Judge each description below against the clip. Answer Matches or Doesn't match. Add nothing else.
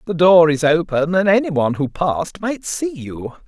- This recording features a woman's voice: Doesn't match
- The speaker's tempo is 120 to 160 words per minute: Doesn't match